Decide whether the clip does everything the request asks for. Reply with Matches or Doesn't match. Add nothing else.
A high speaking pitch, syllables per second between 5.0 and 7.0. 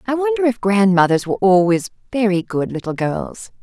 Matches